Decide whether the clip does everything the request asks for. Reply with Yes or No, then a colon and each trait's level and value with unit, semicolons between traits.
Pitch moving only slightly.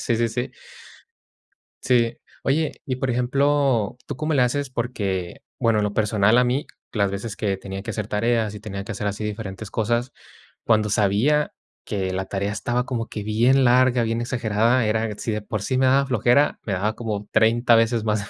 No: average, 3.1 semitones